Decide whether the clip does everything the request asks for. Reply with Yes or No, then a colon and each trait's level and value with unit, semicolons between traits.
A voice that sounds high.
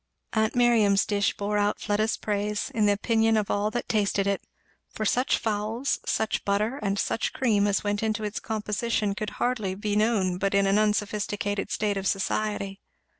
Yes: high, 210 Hz